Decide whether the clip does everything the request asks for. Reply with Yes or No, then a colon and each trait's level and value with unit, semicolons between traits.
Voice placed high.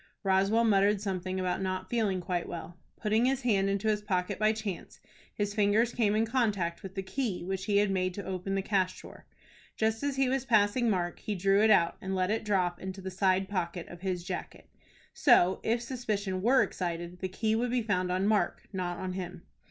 Yes: high, 195 Hz